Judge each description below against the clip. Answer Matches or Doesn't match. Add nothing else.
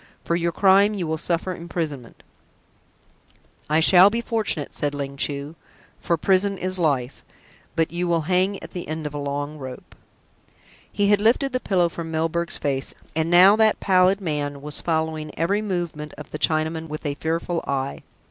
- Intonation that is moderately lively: Matches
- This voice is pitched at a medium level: Matches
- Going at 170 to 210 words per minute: Matches